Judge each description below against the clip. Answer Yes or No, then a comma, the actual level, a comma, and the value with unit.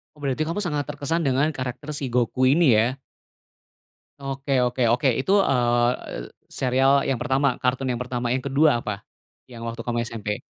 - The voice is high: No, low, 130 Hz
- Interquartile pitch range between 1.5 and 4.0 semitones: Yes, average, 2.8 semitones